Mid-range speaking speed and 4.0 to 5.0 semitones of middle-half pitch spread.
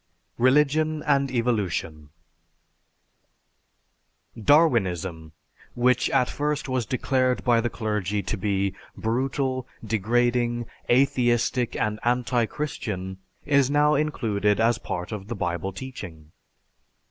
No: slow, 100 wpm; average, 4.5 semitones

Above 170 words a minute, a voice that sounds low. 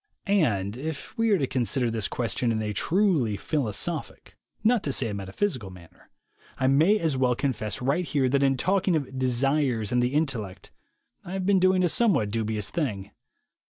Yes: average, 180 wpm; low, 130 Hz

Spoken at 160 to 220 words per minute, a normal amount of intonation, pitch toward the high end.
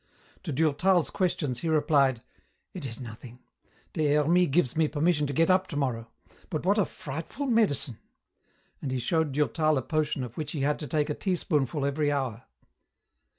No: average, 170 wpm; average, 3.4 semitones; medium, 150 Hz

